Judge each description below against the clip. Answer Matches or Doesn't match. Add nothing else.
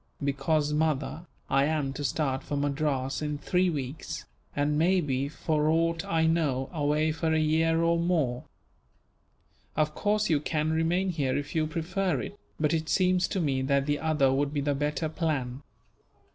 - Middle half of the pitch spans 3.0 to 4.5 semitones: Doesn't match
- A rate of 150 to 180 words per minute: Matches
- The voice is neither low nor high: Matches